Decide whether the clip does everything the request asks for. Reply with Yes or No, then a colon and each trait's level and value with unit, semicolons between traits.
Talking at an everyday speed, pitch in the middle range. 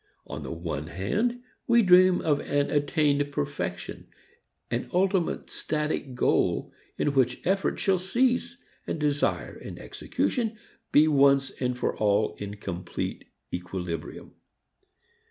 No: slow, 120 wpm; medium, 145 Hz